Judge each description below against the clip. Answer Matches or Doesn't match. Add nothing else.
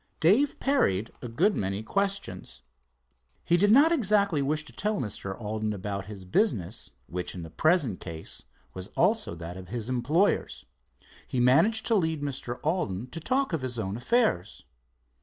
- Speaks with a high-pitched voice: Doesn't match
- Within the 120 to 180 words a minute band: Matches